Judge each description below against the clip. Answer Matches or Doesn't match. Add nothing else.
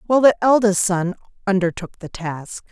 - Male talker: Doesn't match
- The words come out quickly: Doesn't match